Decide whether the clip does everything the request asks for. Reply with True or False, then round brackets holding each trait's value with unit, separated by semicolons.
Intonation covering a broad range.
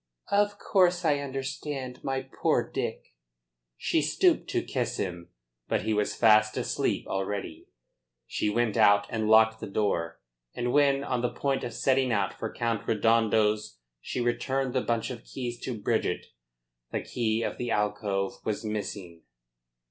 False (4.0 semitones)